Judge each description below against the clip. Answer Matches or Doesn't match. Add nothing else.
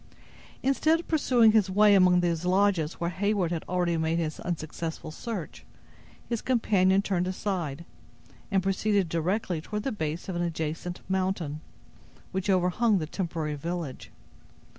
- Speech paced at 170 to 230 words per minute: Doesn't match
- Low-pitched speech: Doesn't match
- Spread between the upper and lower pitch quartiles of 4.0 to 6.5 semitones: Doesn't match